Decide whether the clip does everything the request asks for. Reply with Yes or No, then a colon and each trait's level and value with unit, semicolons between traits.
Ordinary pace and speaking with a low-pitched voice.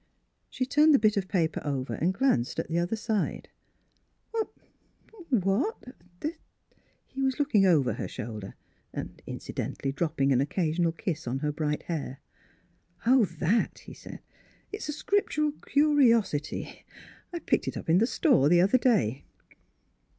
No: average, 160 wpm; high, 190 Hz